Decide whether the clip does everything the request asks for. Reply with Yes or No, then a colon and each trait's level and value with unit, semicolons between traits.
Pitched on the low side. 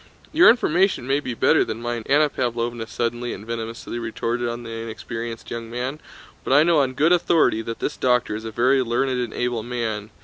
Yes: low, 120 Hz